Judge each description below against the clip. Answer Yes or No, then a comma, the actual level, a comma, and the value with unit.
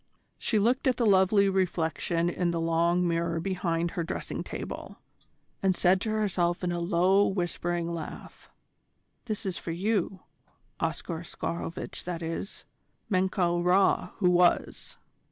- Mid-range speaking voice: Yes, medium, 180 Hz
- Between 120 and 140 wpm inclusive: Yes, slow, 135 wpm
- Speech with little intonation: Yes, narrow, 2.2 semitones